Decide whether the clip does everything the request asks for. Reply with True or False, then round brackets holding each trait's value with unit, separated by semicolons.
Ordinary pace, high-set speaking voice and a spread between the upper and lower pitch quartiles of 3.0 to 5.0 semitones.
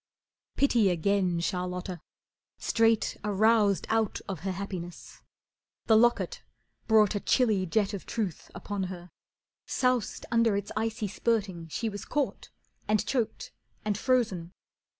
False (125 wpm; 205 Hz; 3.4 semitones)